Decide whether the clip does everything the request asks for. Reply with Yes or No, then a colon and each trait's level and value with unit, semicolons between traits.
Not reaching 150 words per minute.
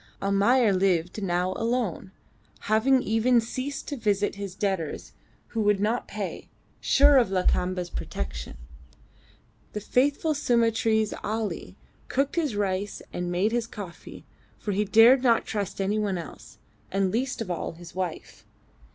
Yes: average, 140 wpm